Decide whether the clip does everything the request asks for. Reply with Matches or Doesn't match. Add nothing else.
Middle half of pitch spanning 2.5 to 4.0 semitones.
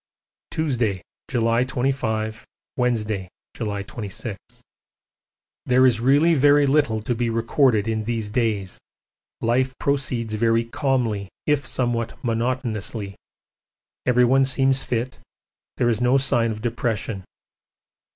Matches